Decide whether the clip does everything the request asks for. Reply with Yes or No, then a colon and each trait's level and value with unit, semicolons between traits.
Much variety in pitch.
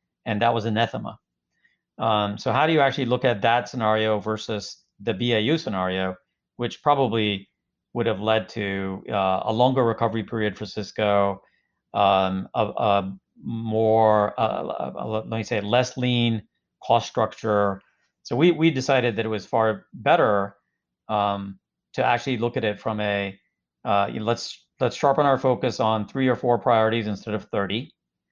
No: average, 3.0 semitones